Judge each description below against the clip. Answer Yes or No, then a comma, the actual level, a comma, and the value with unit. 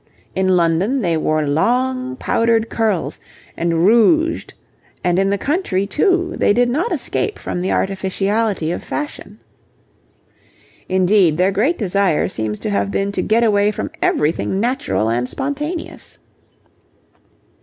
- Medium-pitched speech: No, high, 200 Hz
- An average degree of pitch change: No, wide, 6.3 semitones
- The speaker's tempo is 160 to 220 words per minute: No, slow, 135 wpm